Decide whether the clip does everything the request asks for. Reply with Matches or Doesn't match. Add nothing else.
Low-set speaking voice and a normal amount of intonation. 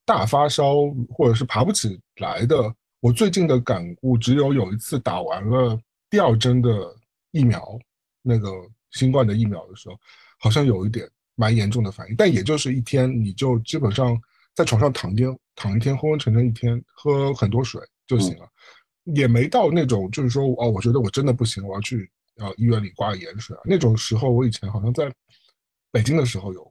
Matches